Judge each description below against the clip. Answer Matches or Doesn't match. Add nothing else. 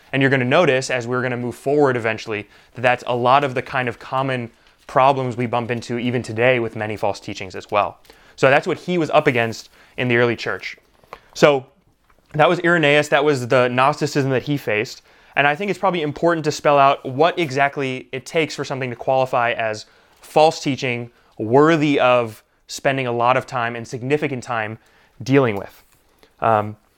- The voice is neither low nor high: Doesn't match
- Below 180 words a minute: Doesn't match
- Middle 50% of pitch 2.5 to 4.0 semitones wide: Matches